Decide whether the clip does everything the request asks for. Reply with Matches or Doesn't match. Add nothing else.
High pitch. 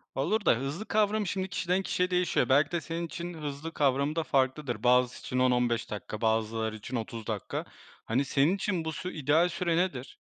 Doesn't match